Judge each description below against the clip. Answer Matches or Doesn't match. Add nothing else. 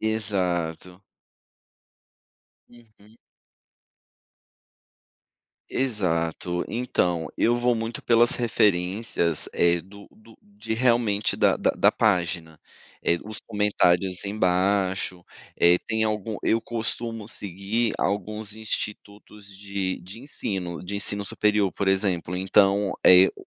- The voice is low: Matches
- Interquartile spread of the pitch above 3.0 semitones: Matches